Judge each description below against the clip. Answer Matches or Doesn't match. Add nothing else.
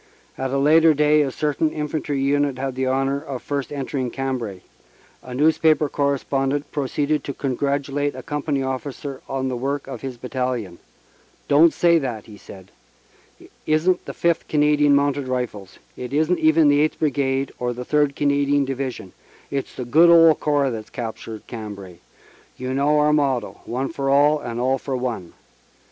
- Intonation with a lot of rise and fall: Doesn't match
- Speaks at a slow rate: Doesn't match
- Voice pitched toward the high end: Doesn't match